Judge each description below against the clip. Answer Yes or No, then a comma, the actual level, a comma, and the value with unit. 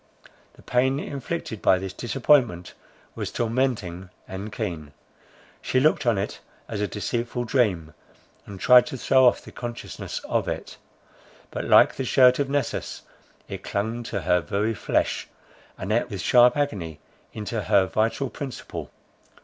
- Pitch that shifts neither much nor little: Yes, average, 4.5 semitones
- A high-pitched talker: No, low, 115 Hz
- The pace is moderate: Yes, average, 150 wpm